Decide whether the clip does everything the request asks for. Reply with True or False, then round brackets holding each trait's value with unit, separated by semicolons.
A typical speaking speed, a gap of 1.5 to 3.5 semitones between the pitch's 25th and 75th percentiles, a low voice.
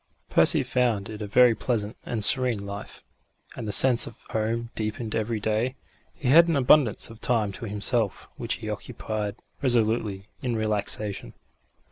True (155 wpm; 2.6 semitones; 110 Hz)